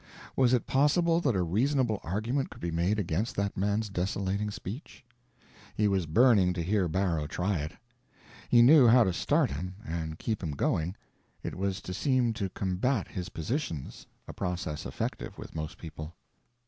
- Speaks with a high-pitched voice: No, low, 100 Hz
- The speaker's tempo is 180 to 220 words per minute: No, average, 165 wpm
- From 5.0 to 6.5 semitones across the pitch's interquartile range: Yes, average, 5.3 semitones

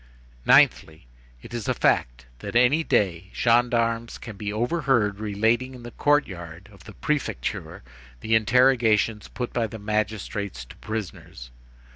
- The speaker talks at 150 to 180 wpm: No, average, 140 wpm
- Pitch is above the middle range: No, low, 110 Hz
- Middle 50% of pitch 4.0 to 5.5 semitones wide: No, average, 3.3 semitones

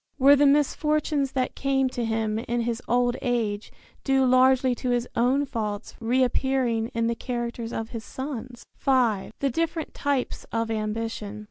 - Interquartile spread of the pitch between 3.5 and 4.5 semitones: No, average, 2.8 semitones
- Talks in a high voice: Yes, high, 245 Hz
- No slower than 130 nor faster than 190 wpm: Yes, average, 155 wpm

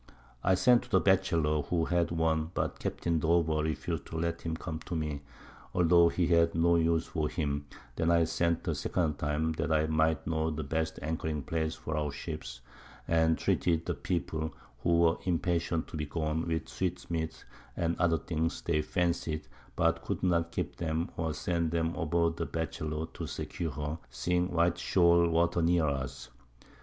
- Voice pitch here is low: Yes, very low, 80 Hz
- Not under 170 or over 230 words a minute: Yes, average, 180 wpm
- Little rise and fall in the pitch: Yes, narrow, 1.5 semitones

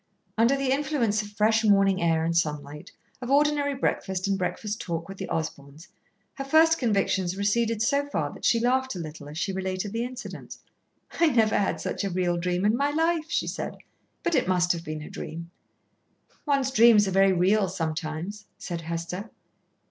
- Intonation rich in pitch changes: Yes, wide, 6.2 semitones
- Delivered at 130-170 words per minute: No, average, 185 wpm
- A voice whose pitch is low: No, high, 200 Hz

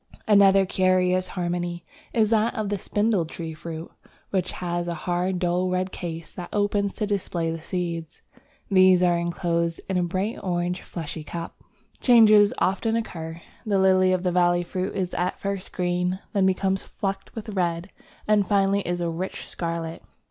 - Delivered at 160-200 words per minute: Yes, average, 170 wpm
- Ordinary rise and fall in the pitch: No, narrow, 2.2 semitones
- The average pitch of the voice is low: No, medium, 185 Hz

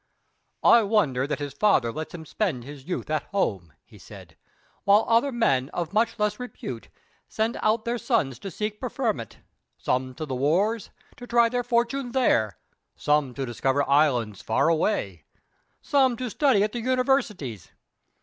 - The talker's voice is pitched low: No, high, 200 Hz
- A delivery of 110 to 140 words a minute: No, average, 160 wpm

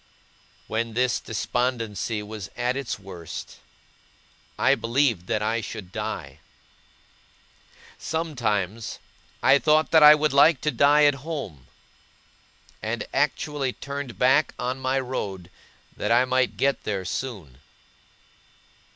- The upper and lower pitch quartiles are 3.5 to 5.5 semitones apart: Yes, average, 4.7 semitones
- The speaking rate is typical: No, slow, 115 wpm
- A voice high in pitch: No, low, 125 Hz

